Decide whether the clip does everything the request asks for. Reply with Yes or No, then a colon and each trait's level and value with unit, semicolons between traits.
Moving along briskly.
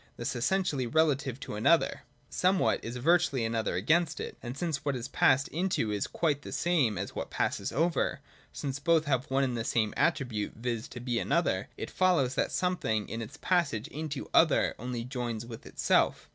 No: average, 195 wpm